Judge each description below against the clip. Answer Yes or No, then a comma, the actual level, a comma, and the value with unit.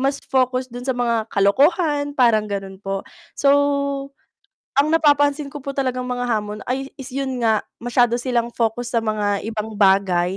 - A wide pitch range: No, average, 4.2 semitones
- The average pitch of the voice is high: Yes, high, 245 Hz